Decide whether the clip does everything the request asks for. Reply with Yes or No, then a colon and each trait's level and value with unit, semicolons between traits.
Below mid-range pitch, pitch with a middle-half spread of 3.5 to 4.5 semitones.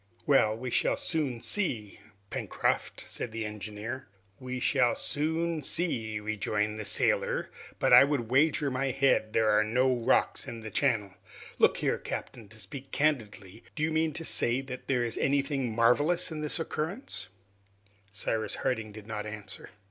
No: low, 125 Hz; average, 4.9 semitones